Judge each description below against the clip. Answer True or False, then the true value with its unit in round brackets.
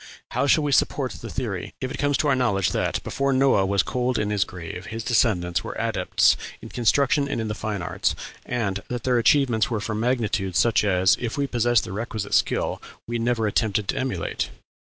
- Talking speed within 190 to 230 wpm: True (205 wpm)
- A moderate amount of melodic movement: True (4.0 semitones)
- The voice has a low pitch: True (115 Hz)